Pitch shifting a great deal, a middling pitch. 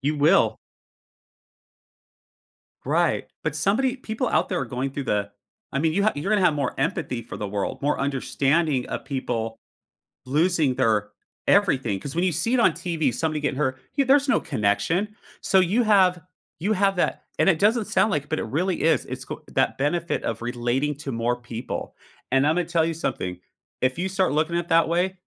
Yes: wide, 6.1 semitones; medium, 155 Hz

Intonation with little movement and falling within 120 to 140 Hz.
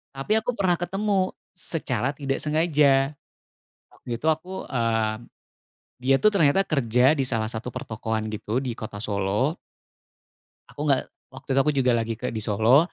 No: wide, 5.6 semitones; low, 135 Hz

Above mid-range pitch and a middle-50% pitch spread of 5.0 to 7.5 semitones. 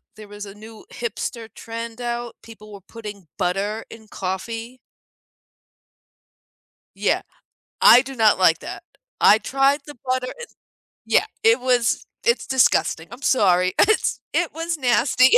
No: high, 230 Hz; average, 3.7 semitones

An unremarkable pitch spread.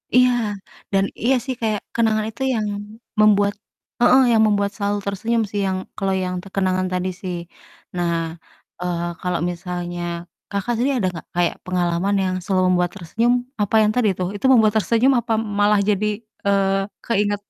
Yes: average, 3.1 semitones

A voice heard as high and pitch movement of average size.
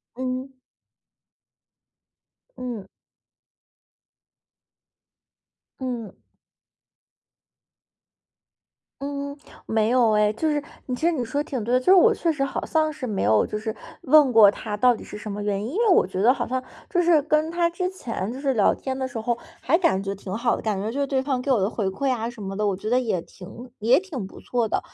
Yes: very high, 250 Hz; average, 5.0 semitones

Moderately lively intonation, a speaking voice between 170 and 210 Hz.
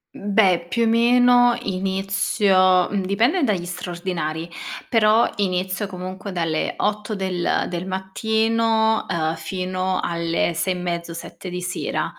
Yes: average, 3.2 semitones; high, 190 Hz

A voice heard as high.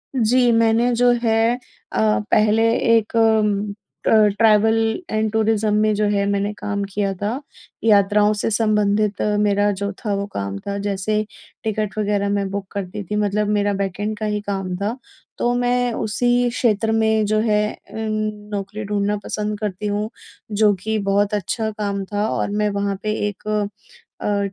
Yes: high, 210 Hz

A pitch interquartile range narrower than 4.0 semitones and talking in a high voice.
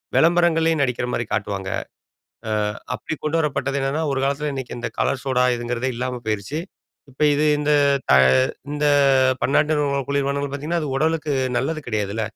No: average, 3.6 semitones; medium, 140 Hz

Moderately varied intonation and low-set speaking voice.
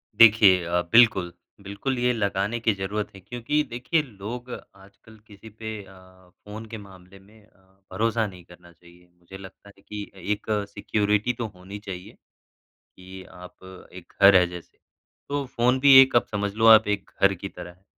Yes: average, 3.2 semitones; low, 100 Hz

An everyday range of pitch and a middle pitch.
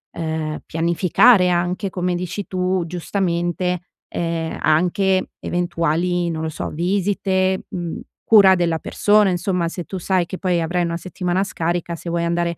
No: narrow, 1.8 semitones; medium, 175 Hz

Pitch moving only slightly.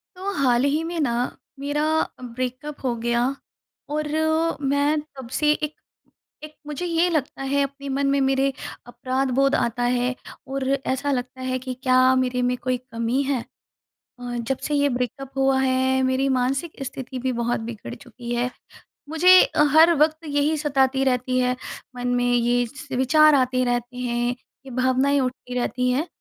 Yes: narrow, 2.2 semitones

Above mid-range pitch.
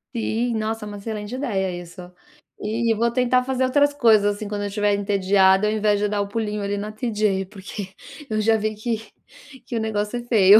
Yes: high, 210 Hz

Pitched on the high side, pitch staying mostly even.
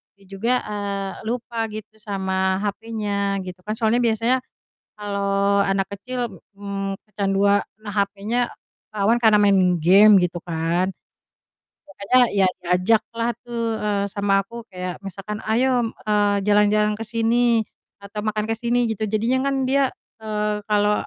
Yes: high, 210 Hz; narrow, 2.3 semitones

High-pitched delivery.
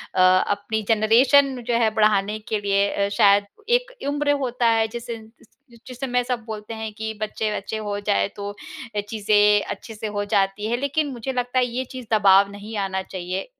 Yes: high, 220 Hz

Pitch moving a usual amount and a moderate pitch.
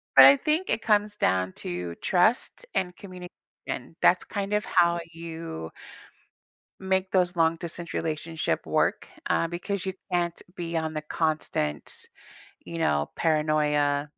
Yes: average, 3.5 semitones; medium, 165 Hz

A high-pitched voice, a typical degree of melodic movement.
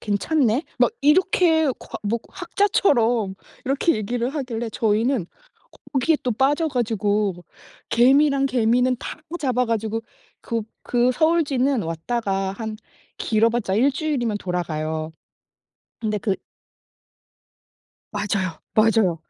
Yes: high, 235 Hz; average, 4.8 semitones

